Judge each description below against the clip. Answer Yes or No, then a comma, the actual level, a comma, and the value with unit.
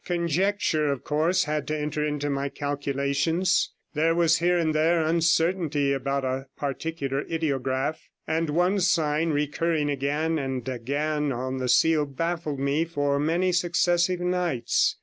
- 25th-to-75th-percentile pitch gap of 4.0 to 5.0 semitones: No, average, 3.2 semitones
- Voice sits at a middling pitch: Yes, medium, 150 Hz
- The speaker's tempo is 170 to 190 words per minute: No, average, 140 wpm